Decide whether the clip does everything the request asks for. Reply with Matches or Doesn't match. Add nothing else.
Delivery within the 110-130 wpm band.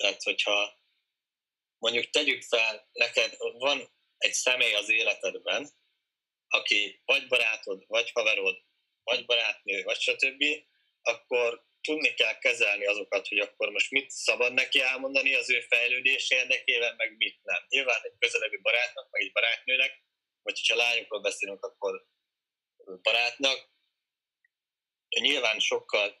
Matches